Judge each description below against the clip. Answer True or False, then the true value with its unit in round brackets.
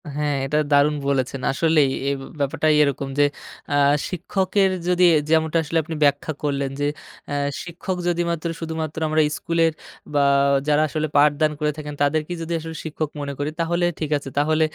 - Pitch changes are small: True (2.3 semitones)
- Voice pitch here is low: False (155 Hz)